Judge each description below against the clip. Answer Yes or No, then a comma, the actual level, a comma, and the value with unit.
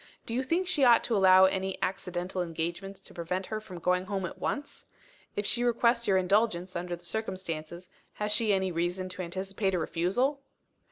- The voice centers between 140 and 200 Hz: Yes, high, 190 Hz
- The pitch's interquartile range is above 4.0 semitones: No, average, 3.4 semitones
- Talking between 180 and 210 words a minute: Yes, average, 185 wpm